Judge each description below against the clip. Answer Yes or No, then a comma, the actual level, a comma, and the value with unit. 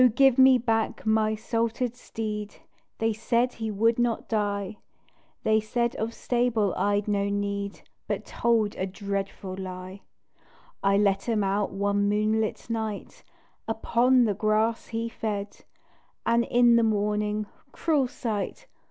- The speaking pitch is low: No, high, 215 Hz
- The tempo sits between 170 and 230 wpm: No, slow, 135 wpm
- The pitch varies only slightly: Yes, narrow, 2.3 semitones